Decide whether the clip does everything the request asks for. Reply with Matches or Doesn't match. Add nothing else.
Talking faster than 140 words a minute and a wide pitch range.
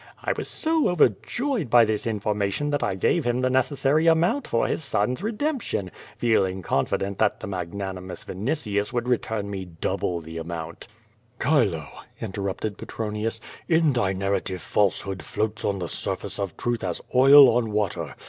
Matches